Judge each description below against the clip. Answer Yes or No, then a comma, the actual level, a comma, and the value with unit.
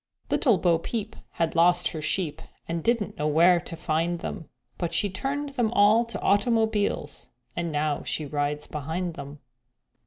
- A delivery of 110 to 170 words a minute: Yes, average, 160 wpm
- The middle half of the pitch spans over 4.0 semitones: Yes, average, 5.0 semitones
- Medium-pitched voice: Yes, medium, 170 Hz